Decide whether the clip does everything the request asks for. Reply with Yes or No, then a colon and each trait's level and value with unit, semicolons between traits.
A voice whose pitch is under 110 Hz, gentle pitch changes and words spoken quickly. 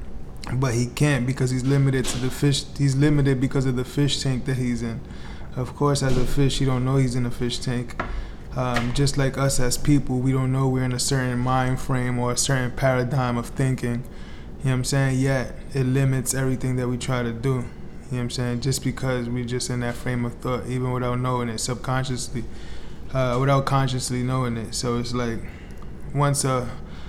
No: low, 125 Hz; narrow, 1.7 semitones; fast, 215 wpm